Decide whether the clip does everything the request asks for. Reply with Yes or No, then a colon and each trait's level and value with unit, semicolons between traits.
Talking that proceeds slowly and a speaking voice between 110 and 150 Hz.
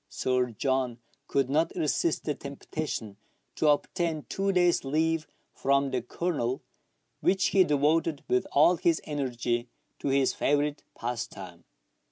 Yes: slow, 130 wpm; medium, 140 Hz